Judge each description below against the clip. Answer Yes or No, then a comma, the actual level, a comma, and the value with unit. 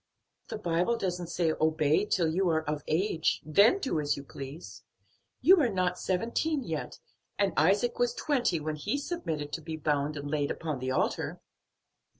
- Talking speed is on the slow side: No, average, 170 wpm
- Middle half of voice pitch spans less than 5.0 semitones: No, average, 5.3 semitones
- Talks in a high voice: No, medium, 165 Hz